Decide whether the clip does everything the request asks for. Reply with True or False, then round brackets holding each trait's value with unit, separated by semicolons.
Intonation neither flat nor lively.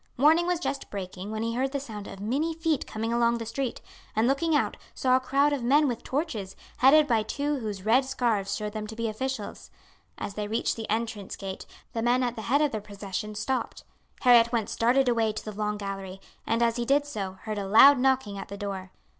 True (4.1 semitones)